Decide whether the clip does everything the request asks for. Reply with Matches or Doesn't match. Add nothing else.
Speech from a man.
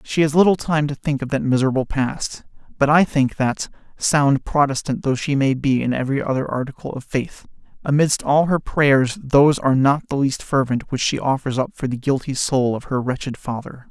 Matches